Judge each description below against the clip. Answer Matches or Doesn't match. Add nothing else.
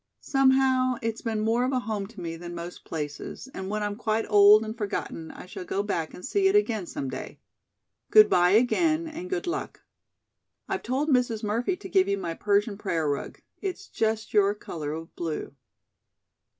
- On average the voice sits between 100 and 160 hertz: Doesn't match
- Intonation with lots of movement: Matches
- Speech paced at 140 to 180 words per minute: Doesn't match